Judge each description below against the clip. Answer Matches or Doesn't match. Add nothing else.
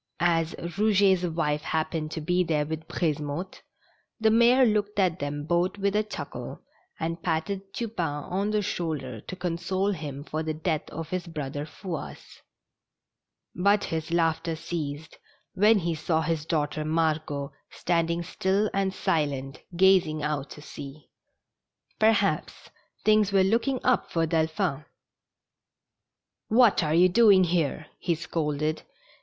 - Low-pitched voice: Doesn't match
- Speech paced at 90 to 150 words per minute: Matches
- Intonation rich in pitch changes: Doesn't match